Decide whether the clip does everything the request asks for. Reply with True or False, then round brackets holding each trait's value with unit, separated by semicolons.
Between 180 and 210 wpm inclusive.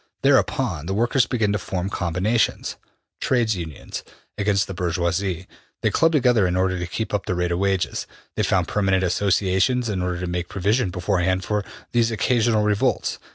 False (170 wpm)